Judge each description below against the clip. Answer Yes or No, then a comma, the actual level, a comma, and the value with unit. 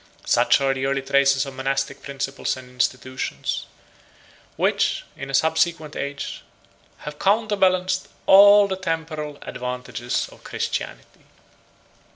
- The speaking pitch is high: No, medium, 140 Hz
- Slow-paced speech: Yes, slow, 120 wpm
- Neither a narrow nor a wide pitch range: Yes, average, 4.7 semitones